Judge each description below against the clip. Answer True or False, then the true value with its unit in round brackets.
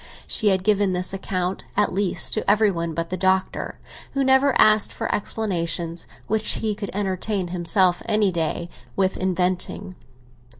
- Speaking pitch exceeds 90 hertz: True (190 Hz)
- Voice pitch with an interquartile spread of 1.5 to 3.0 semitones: True (2.6 semitones)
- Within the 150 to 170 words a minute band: True (155 wpm)